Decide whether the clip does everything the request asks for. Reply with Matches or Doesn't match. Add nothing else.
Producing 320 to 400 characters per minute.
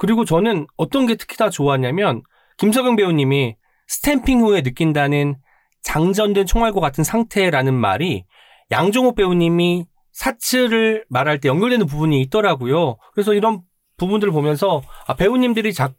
Matches